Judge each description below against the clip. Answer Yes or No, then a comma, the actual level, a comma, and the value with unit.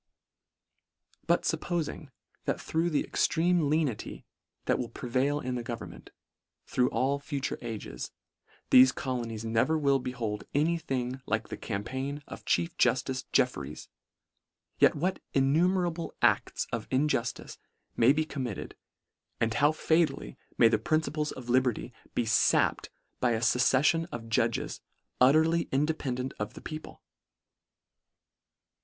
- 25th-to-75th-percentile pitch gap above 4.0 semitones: Yes, average, 4.6 semitones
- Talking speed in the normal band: No, slow, 125 wpm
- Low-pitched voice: Yes, low, 130 Hz